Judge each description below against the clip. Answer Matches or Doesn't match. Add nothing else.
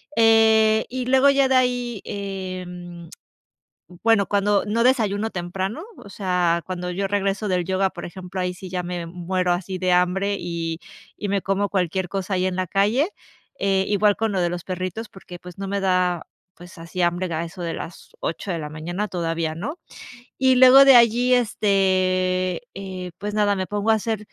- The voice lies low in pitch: Doesn't match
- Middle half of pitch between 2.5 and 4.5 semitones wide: Matches